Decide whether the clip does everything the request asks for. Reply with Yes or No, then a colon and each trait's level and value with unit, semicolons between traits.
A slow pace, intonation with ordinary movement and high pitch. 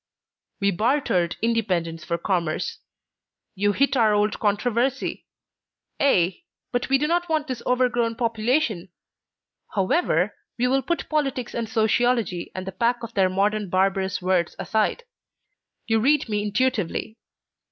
Yes: slow, 130 wpm; average, 4.7 semitones; high, 220 Hz